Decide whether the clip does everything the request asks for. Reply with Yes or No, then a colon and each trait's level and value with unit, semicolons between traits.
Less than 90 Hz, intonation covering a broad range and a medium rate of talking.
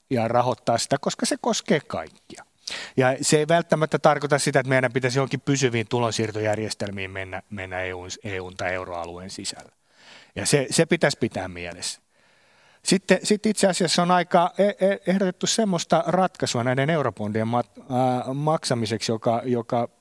No: low, 130 Hz; wide, 7.4 semitones; average, 140 wpm